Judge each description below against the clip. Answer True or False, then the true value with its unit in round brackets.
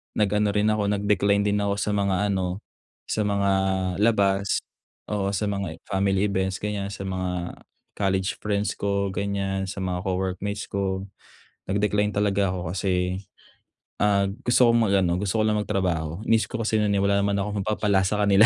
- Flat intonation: True (1.3 semitones)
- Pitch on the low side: True (100 Hz)